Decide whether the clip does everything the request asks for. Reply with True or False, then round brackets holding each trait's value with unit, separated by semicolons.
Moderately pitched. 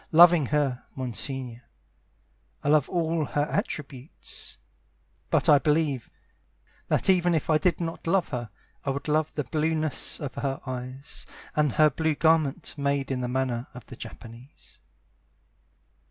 True (145 Hz)